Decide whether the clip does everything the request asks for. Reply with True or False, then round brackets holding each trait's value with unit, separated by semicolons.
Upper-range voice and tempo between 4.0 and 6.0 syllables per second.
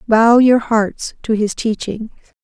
False (225 Hz; 3.7 syllables/s)